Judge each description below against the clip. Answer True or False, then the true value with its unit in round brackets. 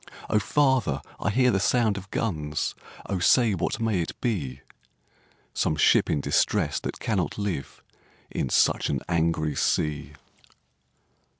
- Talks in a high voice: False (95 Hz)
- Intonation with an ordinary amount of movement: False (6.4 semitones)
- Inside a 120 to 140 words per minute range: True (135 wpm)